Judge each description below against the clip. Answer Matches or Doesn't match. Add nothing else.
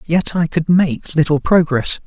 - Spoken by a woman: Doesn't match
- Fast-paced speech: Doesn't match